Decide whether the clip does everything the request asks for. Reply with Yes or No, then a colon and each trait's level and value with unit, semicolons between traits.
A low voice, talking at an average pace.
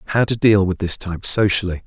No: low, 100 Hz; fast, 225 wpm